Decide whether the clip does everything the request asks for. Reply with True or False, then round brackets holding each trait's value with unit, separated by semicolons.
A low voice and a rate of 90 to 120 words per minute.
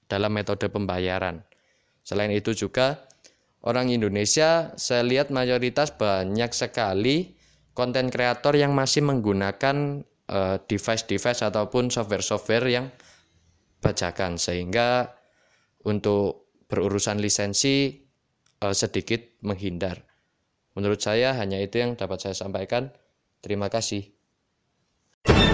True (105 Hz; 95 wpm)